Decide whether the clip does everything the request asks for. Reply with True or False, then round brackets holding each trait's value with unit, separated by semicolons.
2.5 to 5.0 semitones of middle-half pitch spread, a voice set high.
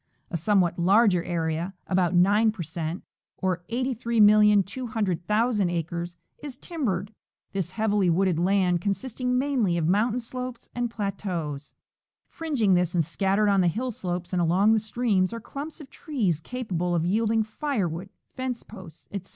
True (4.7 semitones; 200 Hz)